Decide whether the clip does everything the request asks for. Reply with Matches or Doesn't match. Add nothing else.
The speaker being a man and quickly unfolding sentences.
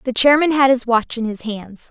Doesn't match